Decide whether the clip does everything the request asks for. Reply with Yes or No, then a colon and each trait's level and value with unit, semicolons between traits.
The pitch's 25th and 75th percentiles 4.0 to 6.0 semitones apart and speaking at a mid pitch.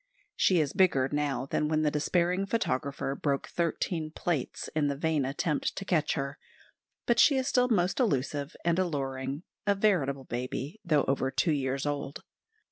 Yes: average, 4.3 semitones; medium, 150 Hz